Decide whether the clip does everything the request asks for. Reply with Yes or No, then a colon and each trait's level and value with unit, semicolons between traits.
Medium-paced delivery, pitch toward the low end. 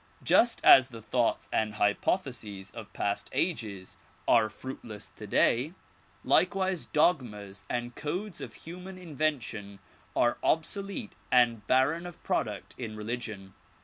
No: slow, 115 wpm; low, 120 Hz